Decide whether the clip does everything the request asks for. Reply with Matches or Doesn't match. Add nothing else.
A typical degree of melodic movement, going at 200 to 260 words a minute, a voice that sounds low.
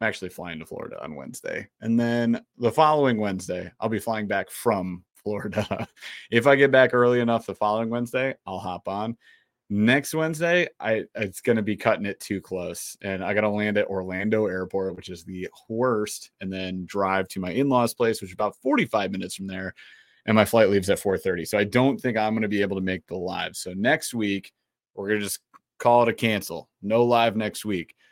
Matches